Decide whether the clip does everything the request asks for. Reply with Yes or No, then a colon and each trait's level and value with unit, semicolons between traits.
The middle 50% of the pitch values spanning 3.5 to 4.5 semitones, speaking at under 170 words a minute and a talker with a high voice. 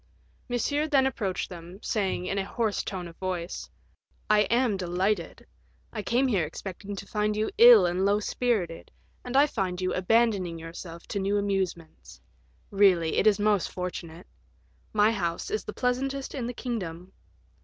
Yes: average, 4.2 semitones; average, 160 wpm; high, 200 Hz